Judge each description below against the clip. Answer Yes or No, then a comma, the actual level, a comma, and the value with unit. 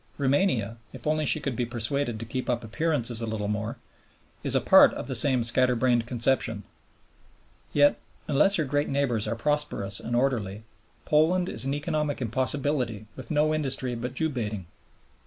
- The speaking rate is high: No, average, 170 wpm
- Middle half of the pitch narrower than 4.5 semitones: Yes, average, 4.1 semitones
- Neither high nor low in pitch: No, low, 130 Hz